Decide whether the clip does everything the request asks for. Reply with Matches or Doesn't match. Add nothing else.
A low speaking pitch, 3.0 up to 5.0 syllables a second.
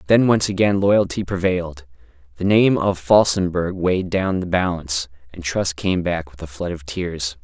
Matches